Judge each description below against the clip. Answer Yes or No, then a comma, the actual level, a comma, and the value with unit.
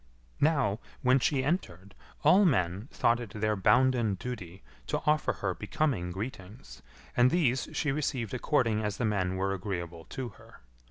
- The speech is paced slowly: No, average, 155 wpm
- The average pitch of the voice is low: Yes, low, 110 Hz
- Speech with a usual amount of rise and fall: No, wide, 5.7 semitones